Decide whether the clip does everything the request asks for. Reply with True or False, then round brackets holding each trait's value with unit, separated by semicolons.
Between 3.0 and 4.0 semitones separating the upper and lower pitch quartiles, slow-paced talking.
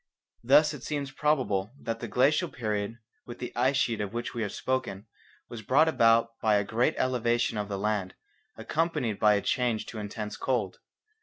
False (3.7 semitones; 180 wpm)